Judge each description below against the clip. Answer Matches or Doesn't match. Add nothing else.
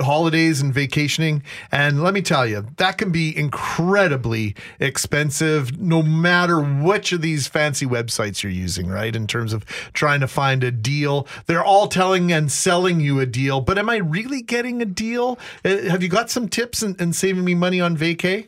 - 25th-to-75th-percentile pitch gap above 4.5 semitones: Matches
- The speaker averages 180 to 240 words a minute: Matches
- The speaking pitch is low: Doesn't match